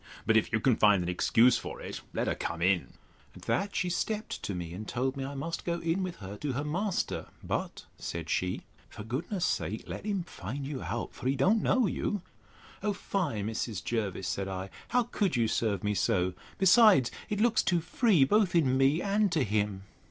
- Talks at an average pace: No, fast, 210 wpm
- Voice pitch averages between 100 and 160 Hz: Yes, low, 135 Hz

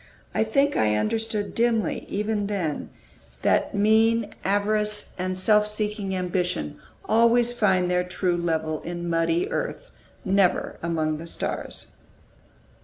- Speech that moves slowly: Yes, slow, 120 wpm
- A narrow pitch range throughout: No, average, 4.0 semitones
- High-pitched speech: Yes, high, 200 Hz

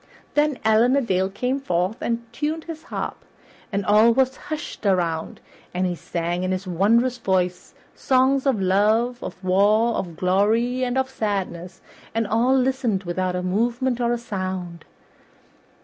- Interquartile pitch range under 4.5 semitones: No, average, 5.2 semitones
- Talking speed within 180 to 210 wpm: No, average, 155 wpm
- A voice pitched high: Yes, high, 215 Hz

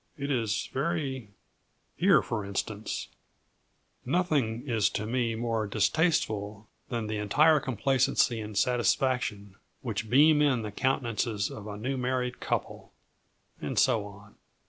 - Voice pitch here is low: Yes, low, 115 Hz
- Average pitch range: Yes, average, 3.9 semitones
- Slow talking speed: Yes, slow, 125 wpm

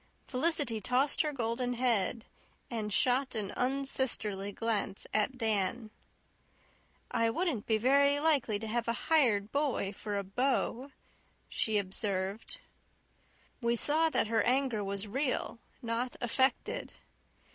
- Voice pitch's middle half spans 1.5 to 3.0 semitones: No, average, 3.9 semitones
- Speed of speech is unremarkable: No, slow, 125 wpm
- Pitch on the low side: No, high, 235 Hz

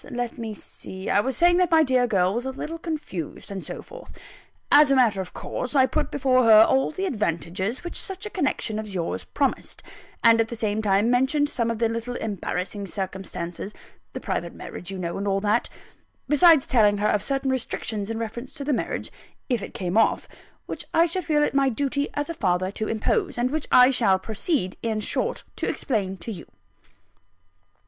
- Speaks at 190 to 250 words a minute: Yes, average, 200 wpm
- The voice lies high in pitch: Yes, high, 230 Hz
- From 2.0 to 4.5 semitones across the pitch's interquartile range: No, wide, 5.5 semitones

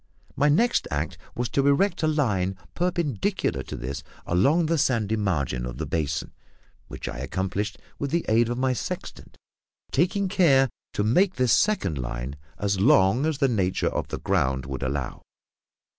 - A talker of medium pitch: No, low, 110 Hz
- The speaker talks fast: No, average, 165 wpm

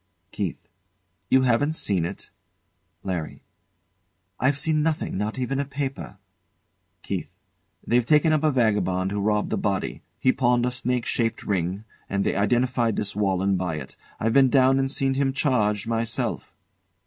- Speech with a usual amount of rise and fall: Yes, average, 4.9 semitones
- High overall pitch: No, low, 120 Hz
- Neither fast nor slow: Yes, average, 155 wpm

